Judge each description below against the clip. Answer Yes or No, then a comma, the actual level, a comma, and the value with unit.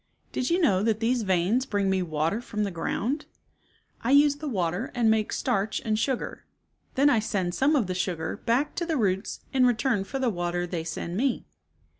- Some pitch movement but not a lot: No, wide, 5.9 semitones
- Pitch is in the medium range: No, high, 220 Hz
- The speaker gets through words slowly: No, average, 200 wpm